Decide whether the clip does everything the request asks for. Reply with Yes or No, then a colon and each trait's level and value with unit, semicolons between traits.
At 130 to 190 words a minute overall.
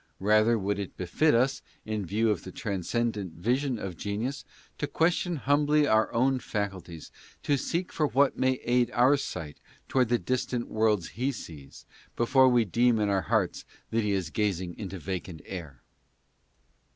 Yes: average, 165 wpm